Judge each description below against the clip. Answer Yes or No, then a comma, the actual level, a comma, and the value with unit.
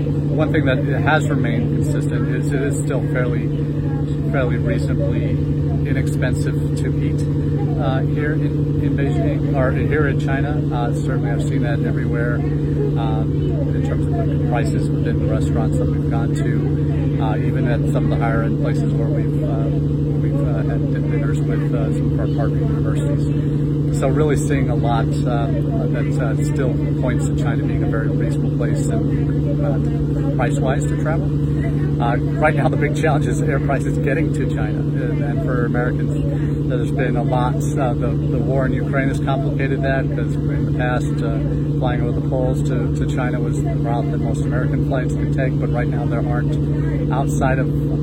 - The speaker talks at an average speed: Yes, average, 180 wpm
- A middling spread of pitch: No, narrow, 0.5 semitones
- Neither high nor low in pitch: Yes, medium, 145 Hz